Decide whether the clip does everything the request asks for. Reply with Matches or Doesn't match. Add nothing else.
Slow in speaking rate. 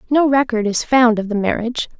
Doesn't match